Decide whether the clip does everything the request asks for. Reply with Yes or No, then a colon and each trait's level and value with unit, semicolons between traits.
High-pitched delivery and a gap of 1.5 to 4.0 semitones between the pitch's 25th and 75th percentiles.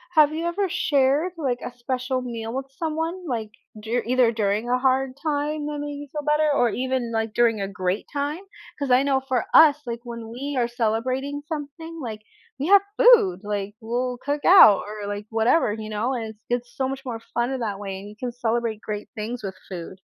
No: very high, 250 Hz; average, 4.5 semitones